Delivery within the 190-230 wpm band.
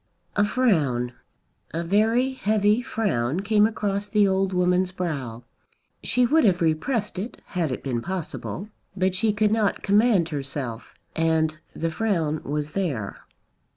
No: average, 140 wpm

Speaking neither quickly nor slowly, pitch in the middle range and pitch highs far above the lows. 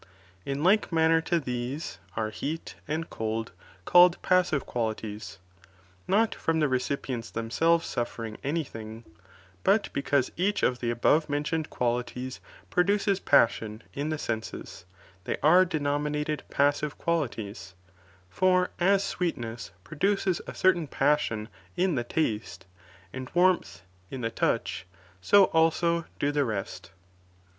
No: slow, 125 wpm; medium, 145 Hz; wide, 6.2 semitones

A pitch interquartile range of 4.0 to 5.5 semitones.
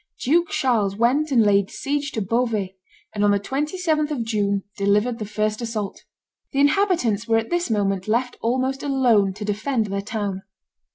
Yes: average, 4.8 semitones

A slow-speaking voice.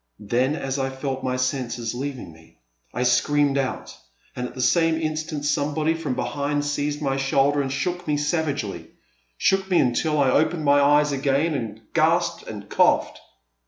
No: average, 175 wpm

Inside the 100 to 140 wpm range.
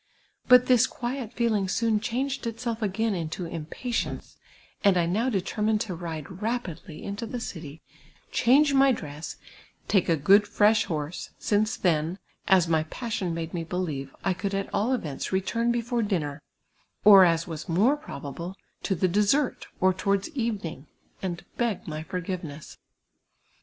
No: average, 150 wpm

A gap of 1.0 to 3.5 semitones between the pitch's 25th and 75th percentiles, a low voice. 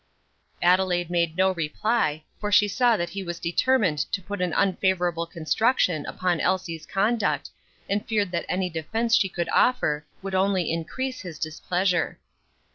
No: average, 3.2 semitones; medium, 185 Hz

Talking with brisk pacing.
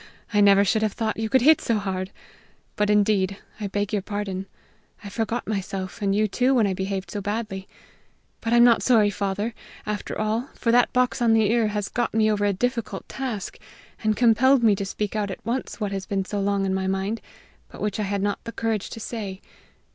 Yes: fast, 215 wpm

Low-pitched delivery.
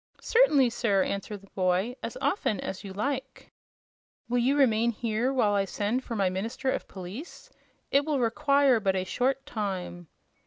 No: high, 225 Hz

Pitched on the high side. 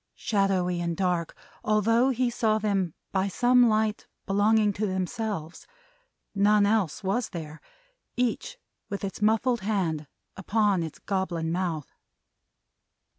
Yes: high, 200 Hz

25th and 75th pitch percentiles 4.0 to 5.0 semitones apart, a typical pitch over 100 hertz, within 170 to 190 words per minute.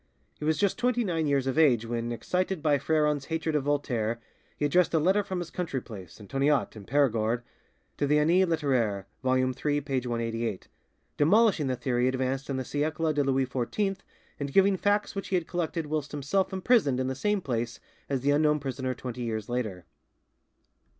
Yes: average, 4.6 semitones; medium, 140 Hz; average, 185 wpm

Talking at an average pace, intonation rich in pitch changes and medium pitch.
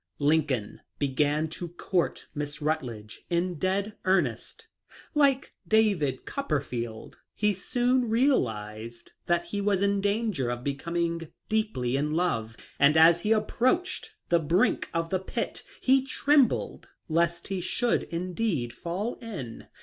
No: slow, 125 wpm; wide, 6.7 semitones; medium, 170 Hz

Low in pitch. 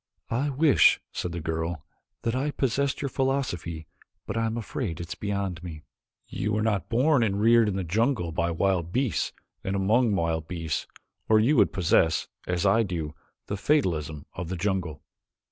Yes: low, 100 Hz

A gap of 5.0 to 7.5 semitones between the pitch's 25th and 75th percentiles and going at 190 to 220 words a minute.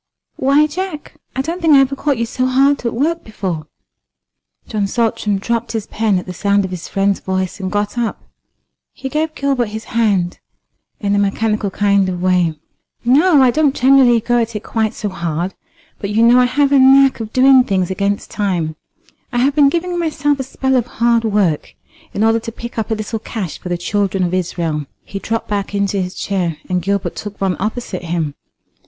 Yes: average, 5.3 semitones; average, 200 wpm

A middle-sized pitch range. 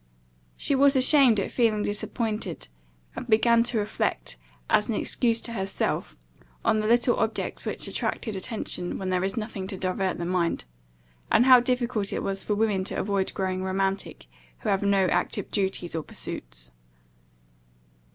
Yes: average, 3.5 semitones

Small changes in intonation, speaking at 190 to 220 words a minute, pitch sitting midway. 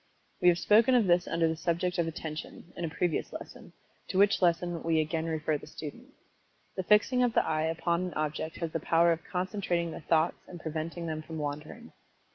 Yes: narrow, 2.1 semitones; fast, 205 wpm; medium, 170 Hz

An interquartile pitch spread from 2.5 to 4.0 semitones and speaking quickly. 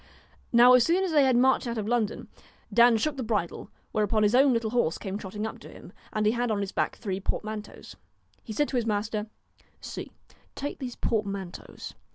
Yes: average, 2.9 semitones; fast, 210 wpm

